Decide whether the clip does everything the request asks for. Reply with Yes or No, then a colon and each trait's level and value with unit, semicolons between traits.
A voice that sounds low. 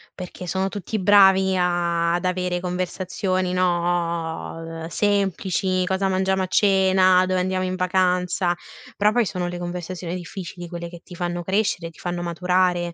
No: medium, 180 Hz